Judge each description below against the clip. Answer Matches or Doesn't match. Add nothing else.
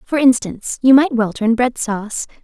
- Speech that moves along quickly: Doesn't match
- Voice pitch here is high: Matches